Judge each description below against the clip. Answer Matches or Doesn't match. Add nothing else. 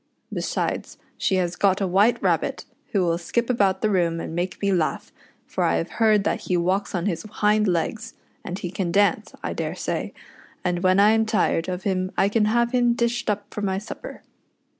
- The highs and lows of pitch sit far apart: Doesn't match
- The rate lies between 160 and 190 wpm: Doesn't match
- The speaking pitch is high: Matches